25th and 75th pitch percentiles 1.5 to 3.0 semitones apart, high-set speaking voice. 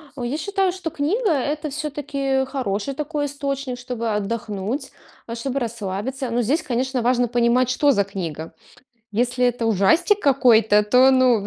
No: average, 3.7 semitones; very high, 255 Hz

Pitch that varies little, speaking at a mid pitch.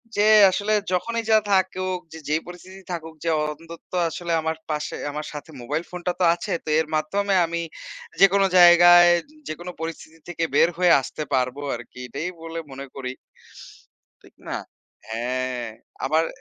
No: average, 3.1 semitones; medium, 165 Hz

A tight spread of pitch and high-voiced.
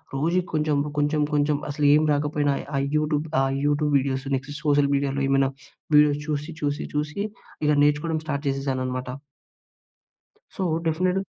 No: narrow, 1.4 semitones; medium, 145 Hz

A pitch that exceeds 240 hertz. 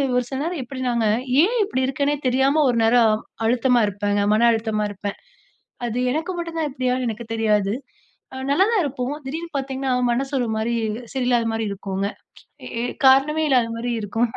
Yes: very high, 250 Hz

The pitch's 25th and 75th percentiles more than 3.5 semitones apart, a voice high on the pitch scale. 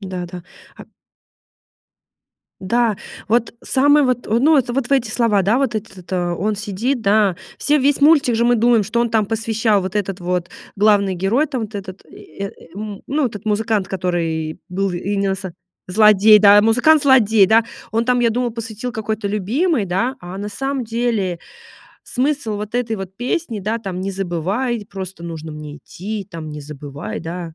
Yes: average, 4.1 semitones; high, 210 Hz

